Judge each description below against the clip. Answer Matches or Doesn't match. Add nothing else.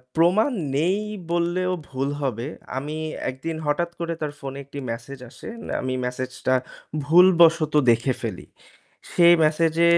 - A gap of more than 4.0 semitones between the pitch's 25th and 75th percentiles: Matches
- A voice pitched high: Doesn't match